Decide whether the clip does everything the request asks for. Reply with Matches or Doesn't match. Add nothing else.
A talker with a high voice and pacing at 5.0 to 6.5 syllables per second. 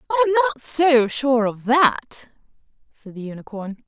Doesn't match